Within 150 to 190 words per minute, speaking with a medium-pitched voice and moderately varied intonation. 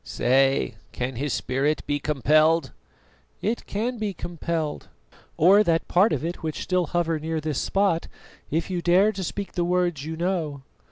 Yes: average, 165 wpm; medium, 165 Hz; average, 3.5 semitones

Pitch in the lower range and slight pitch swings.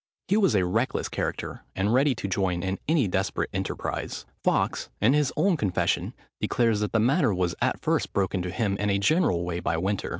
No: low, 100 Hz; wide, 5.6 semitones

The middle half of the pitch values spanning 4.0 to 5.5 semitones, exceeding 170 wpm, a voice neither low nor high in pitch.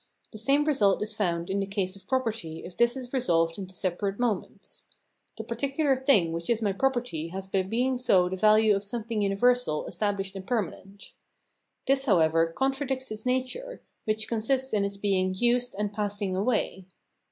No: average, 4.6 semitones; average, 180 wpm; high, 210 Hz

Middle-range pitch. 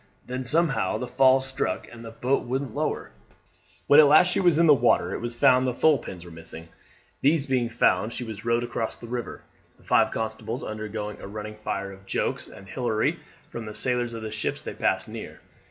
No: low, 120 Hz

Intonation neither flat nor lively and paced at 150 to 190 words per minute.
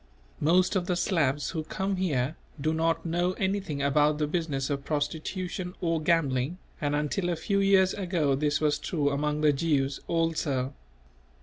Yes: average, 3.5 semitones; average, 165 wpm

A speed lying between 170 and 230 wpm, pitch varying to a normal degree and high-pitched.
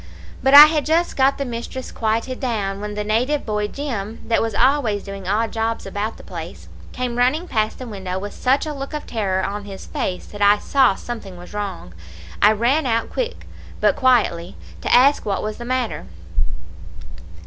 Yes: average, 190 wpm; average, 4.2 semitones; high, 225 Hz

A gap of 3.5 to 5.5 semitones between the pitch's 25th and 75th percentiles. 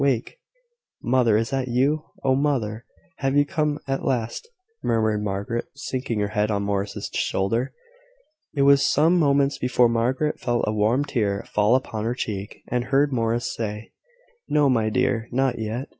Yes: average, 3.9 semitones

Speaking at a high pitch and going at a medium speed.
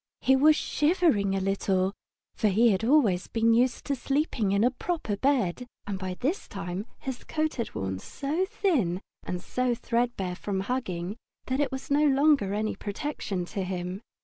Yes: high, 230 Hz; average, 170 wpm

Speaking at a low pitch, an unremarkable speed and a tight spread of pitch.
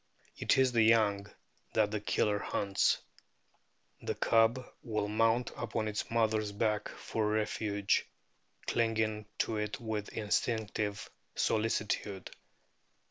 No: low, 110 Hz; slow, 115 wpm; narrow, 1.4 semitones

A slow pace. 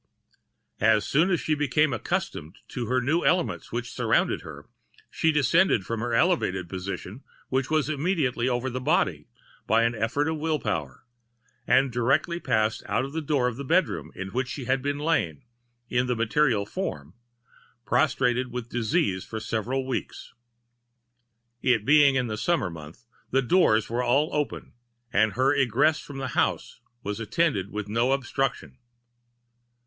No: average, 160 wpm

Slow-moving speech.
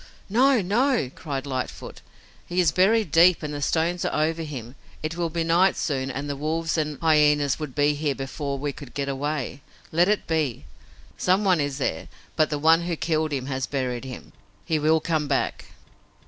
No: average, 190 wpm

